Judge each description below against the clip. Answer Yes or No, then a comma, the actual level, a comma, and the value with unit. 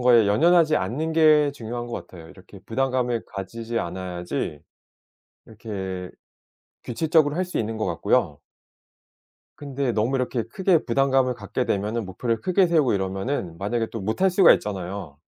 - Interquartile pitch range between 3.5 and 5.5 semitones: No, wide, 6.4 semitones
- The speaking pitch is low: Yes, low, 115 Hz